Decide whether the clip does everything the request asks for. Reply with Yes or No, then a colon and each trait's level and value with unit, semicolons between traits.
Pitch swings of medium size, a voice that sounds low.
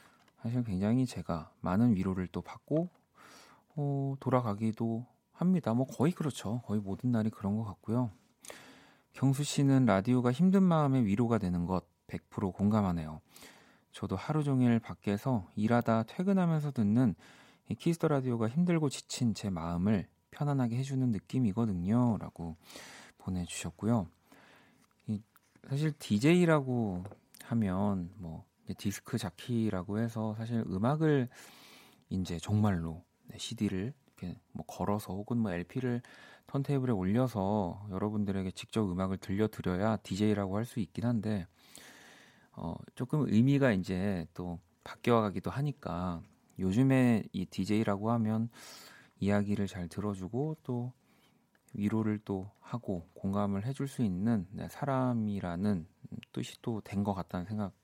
Yes: average, 4.7 semitones; low, 110 Hz